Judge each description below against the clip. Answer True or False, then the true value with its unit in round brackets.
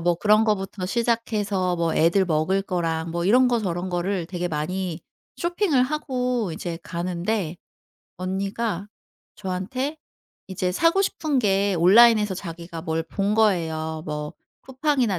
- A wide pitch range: False (4.8 semitones)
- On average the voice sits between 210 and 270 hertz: False (190 Hz)